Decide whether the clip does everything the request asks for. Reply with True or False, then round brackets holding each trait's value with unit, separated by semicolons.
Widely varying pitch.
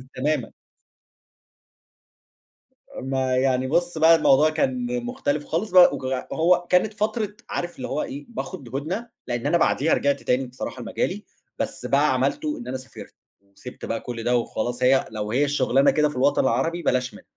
True (6.2 semitones)